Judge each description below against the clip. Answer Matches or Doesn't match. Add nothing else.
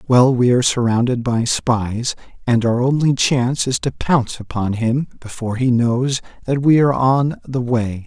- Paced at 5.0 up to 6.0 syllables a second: Doesn't match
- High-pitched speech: Doesn't match